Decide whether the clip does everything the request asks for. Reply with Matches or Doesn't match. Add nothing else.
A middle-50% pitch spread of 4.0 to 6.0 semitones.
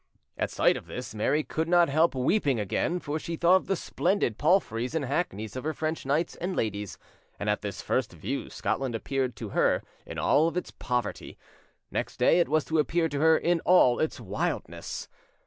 Matches